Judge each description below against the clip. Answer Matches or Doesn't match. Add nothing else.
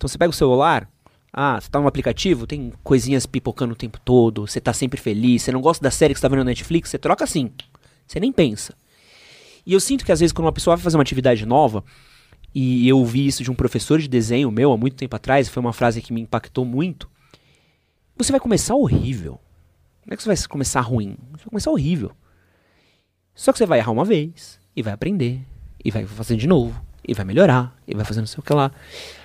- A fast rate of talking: Matches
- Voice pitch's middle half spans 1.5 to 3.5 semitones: Doesn't match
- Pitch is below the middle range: Matches